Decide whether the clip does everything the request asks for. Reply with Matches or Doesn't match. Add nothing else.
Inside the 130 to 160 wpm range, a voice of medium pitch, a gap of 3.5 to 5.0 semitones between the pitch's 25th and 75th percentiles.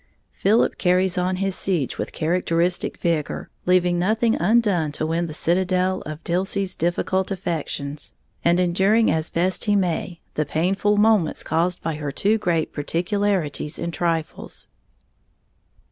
Doesn't match